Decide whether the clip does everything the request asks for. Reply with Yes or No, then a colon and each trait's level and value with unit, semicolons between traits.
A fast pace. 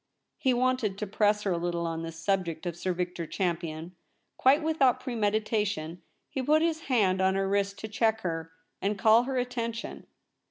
No: average, 185 wpm